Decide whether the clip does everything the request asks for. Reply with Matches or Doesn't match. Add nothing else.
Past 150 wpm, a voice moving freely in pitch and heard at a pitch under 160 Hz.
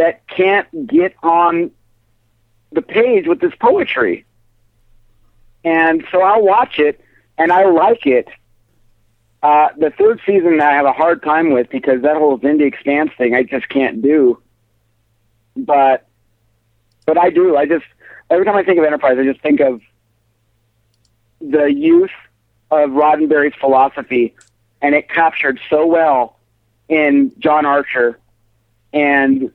Doesn't match